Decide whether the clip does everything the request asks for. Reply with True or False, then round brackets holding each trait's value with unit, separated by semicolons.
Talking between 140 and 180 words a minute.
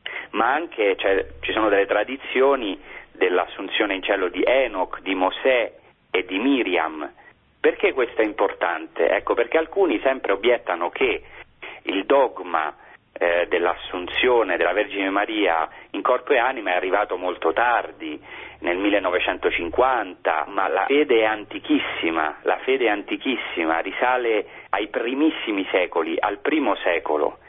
False (130 wpm)